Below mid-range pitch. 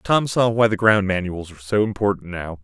Yes: low, 100 Hz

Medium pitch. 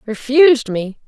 No: high, 245 Hz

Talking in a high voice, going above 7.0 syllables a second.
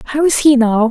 No: very high, 260 Hz; 6.4 syllables/s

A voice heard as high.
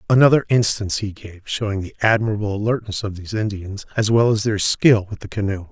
No: low, 105 Hz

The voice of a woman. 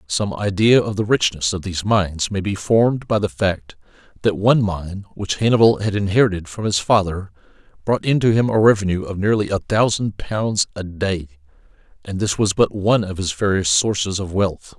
No: male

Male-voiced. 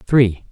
Yes: male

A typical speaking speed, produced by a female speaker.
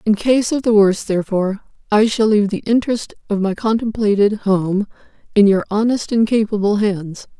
Yes: average, 170 wpm; female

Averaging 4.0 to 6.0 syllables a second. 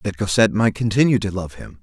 No: 6.4 syllables/s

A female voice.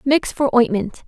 Yes: female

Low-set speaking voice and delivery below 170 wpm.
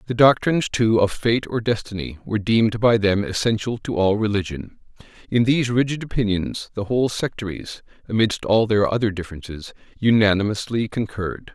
Yes: low, 110 Hz; average, 150 wpm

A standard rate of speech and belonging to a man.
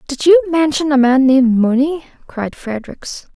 No: average, 160 wpm; female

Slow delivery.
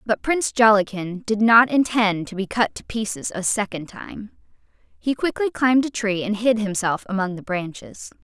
No: average, 180 wpm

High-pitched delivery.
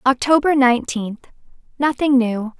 Yes: very high, 255 Hz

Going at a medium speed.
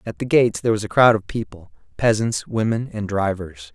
No: fast, 210 wpm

